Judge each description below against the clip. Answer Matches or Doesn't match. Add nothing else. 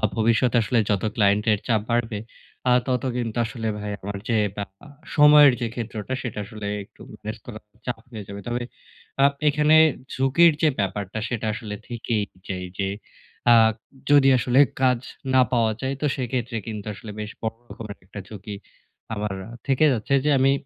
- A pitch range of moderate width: Matches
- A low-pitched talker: Matches